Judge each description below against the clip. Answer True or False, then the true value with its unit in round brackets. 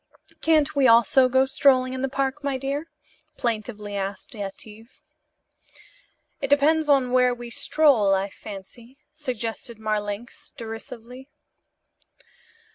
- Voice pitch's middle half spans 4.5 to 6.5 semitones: False (3.9 semitones)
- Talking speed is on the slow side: True (115 wpm)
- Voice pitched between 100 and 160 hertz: False (250 Hz)